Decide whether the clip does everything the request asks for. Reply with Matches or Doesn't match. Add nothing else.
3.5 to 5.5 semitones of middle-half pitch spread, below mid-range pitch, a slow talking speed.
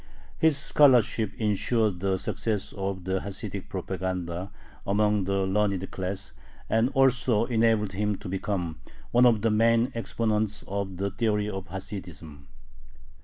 Doesn't match